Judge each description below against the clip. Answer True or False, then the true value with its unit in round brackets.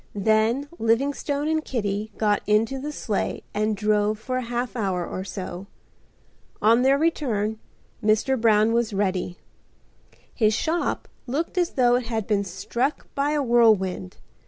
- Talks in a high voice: True (225 Hz)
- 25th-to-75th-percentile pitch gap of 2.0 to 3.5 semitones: False (4.2 semitones)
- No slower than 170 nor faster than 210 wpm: False (145 wpm)